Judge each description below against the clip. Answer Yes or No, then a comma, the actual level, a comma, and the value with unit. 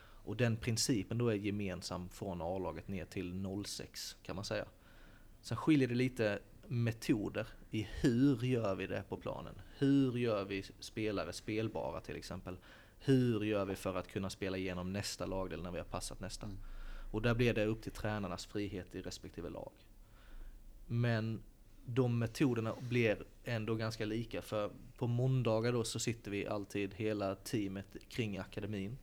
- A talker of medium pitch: No, low, 105 Hz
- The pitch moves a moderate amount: Yes, average, 3.1 semitones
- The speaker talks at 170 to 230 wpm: No, average, 160 wpm